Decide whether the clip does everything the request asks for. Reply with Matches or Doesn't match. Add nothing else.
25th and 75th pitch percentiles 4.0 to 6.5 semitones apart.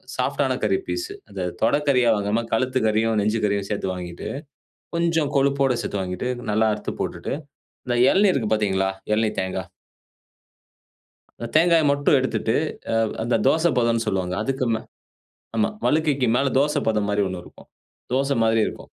Matches